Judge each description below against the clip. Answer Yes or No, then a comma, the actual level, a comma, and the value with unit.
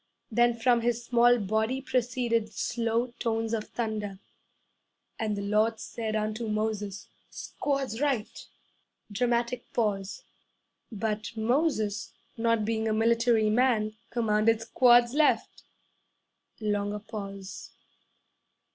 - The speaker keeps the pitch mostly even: Yes, narrow, 2.0 semitones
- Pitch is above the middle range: Yes, high, 225 Hz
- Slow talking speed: Yes, slow, 100 wpm